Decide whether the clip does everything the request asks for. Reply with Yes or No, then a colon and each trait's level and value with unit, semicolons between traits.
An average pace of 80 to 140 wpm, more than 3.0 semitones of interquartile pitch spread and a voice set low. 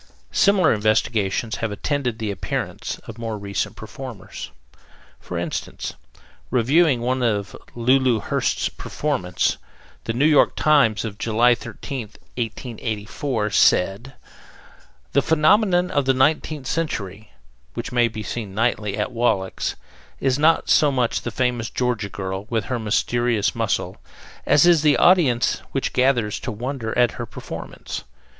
Yes: slow, 135 wpm; average, 3.9 semitones; low, 120 Hz